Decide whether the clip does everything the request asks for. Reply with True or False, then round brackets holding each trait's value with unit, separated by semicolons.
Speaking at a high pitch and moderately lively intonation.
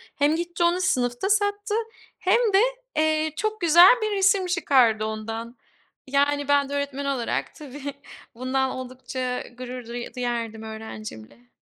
False (275 Hz; 6.0 semitones)